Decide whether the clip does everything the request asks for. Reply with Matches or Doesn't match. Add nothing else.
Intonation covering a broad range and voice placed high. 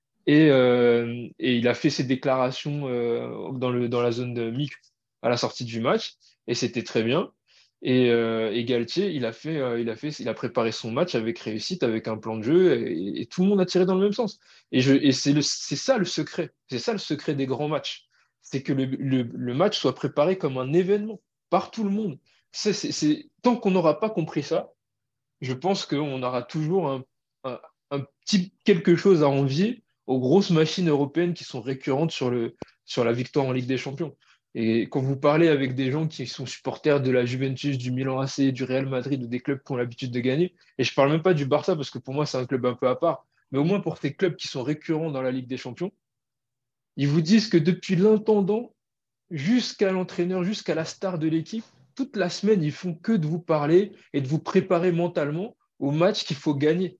Doesn't match